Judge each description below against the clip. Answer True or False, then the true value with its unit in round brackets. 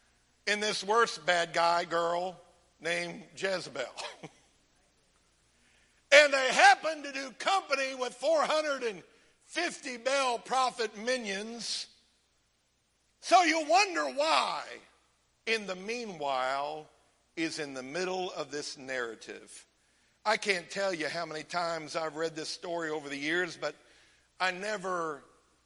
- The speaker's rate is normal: False (115 wpm)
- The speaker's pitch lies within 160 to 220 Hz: True (185 Hz)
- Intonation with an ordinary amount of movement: False (7.6 semitones)